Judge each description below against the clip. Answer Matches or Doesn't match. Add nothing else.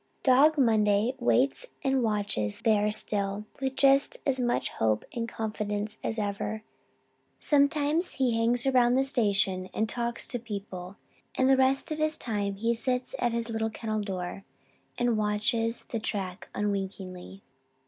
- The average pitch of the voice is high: Matches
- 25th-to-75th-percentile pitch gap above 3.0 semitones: Matches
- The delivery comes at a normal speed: Matches